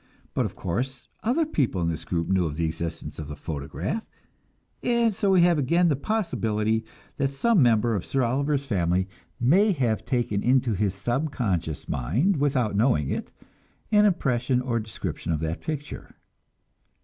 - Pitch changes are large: Yes, wide, 8.0 semitones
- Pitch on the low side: Yes, low, 120 Hz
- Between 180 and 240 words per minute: No, average, 160 wpm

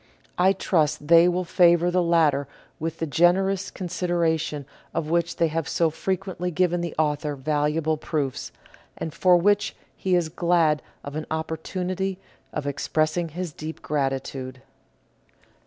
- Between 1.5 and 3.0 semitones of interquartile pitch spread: Yes, average, 2.7 semitones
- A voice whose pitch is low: No, medium, 165 Hz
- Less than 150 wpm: Yes, average, 140 wpm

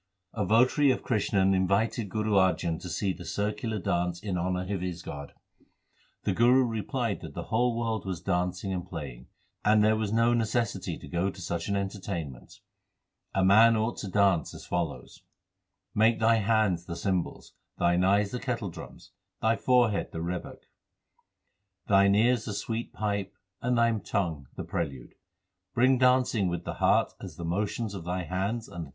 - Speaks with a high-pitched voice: No, low, 100 Hz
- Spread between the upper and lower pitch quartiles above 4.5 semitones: No, average, 4.1 semitones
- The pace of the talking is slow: No, average, 145 wpm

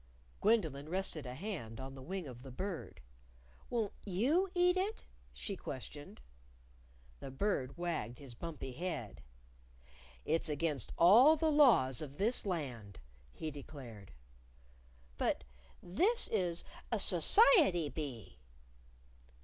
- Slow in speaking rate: Yes, slow, 115 wpm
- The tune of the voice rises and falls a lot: Yes, wide, 7.8 semitones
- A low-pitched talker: No, medium, 165 Hz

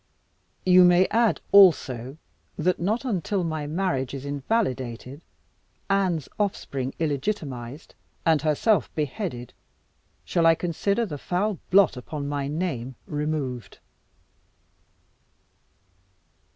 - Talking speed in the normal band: No, slow, 100 wpm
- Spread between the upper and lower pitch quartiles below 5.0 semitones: No, wide, 5.4 semitones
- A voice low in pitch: No, medium, 155 Hz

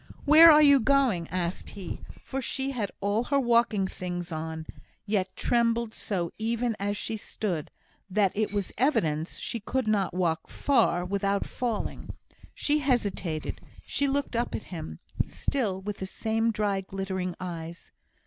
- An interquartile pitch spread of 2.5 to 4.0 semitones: No, average, 4.6 semitones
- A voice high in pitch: Yes, high, 205 Hz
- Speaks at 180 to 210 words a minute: No, average, 150 wpm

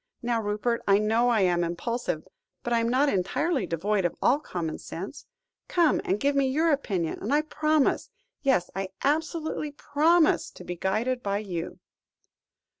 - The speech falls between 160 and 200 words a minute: Yes, average, 165 wpm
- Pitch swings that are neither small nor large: No, wide, 7.1 semitones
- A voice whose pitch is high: Yes, high, 235 Hz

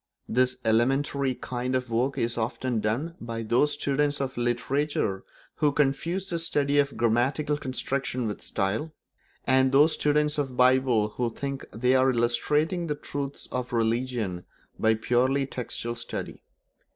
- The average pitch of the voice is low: Yes, low, 130 Hz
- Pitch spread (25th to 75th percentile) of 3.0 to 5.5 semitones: Yes, average, 3.4 semitones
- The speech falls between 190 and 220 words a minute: No, average, 145 wpm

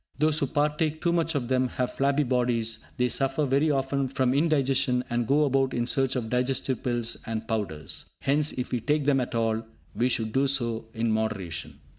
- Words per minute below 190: No, average, 195 wpm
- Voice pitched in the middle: No, low, 130 Hz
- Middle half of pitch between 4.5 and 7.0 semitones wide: No, average, 3.0 semitones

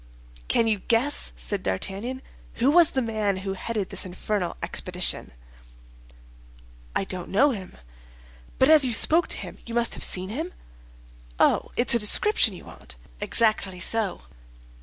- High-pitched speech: Yes, high, 220 Hz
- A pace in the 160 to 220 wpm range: No, average, 150 wpm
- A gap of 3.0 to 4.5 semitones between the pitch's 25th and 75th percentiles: No, average, 4.9 semitones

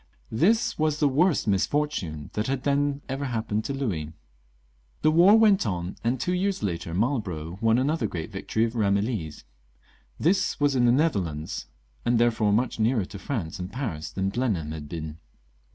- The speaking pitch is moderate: No, low, 115 Hz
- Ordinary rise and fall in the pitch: No, wide, 7.6 semitones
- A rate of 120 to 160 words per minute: No, average, 170 wpm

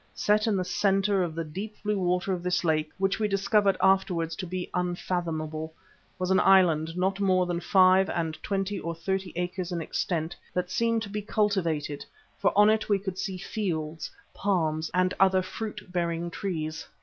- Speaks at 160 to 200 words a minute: Yes, average, 180 wpm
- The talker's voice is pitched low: No, medium, 185 Hz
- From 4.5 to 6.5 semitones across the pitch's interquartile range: No, average, 2.7 semitones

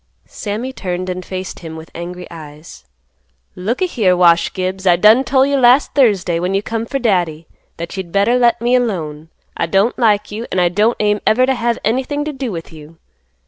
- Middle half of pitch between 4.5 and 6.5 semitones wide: Yes, average, 5.3 semitones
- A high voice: Yes, high, 200 Hz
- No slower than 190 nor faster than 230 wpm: Yes, fast, 205 wpm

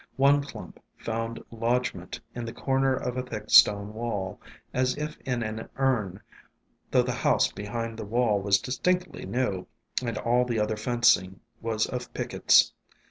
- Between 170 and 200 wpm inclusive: No, average, 160 wpm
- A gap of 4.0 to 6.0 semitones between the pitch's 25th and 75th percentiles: No, average, 3.1 semitones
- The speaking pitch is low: Yes, low, 115 Hz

